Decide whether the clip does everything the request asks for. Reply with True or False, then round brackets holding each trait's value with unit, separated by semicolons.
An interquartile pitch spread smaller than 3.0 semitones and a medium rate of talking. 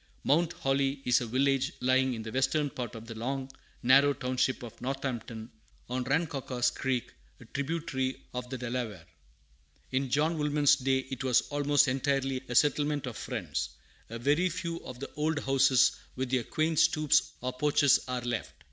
True (2.5 semitones; 165 wpm)